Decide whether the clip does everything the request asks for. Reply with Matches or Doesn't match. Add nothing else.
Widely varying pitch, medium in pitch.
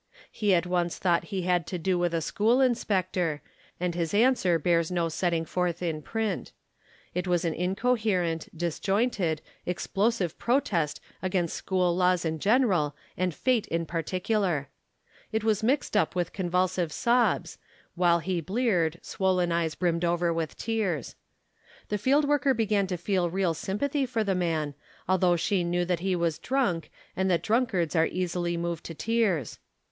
Doesn't match